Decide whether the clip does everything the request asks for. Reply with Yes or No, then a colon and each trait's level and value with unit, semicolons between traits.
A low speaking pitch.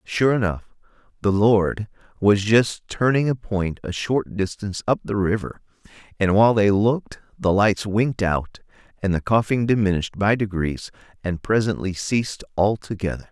Yes: low, 105 Hz